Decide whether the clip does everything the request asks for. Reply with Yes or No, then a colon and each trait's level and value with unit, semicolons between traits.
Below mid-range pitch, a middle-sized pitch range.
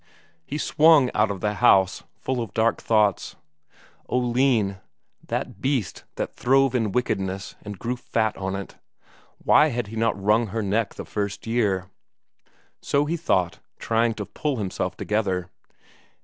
Yes: low, 110 Hz; average, 4.0 semitones